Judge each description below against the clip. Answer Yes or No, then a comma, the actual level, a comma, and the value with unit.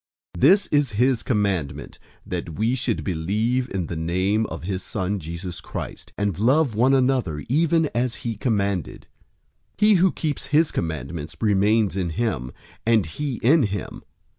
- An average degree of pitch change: No, wide, 6.3 semitones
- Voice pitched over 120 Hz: No, low, 105 Hz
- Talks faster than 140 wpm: Yes, average, 160 wpm